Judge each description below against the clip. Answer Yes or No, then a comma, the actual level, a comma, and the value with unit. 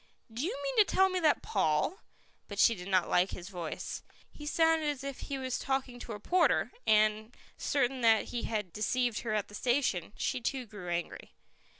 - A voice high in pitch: Yes, high, 240 Hz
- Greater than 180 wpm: Yes, fast, 205 wpm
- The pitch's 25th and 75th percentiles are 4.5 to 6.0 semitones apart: Yes, wide, 5.4 semitones